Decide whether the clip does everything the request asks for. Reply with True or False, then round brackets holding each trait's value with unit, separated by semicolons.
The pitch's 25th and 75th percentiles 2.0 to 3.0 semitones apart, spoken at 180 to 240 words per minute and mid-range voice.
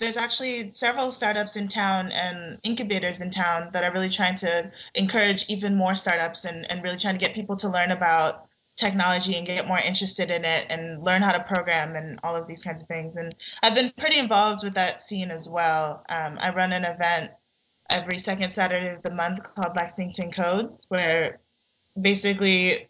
True (2.7 semitones; 195 wpm; 180 Hz)